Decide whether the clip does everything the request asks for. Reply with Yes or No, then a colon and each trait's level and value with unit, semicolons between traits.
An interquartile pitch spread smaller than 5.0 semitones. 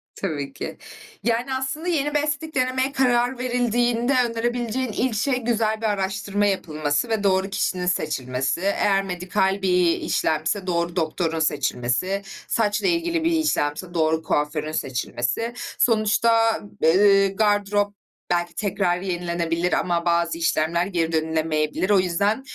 No: wide, 5.6 semitones